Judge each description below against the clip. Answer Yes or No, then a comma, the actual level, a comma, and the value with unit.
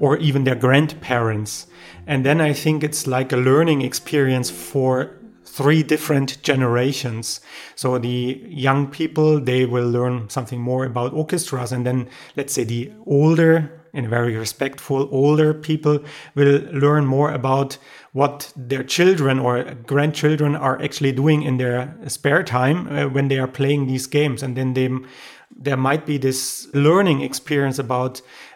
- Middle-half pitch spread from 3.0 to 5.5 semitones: No, narrow, 2.6 semitones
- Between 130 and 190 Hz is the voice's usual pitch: Yes, low, 135 Hz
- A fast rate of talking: No, average, 150 wpm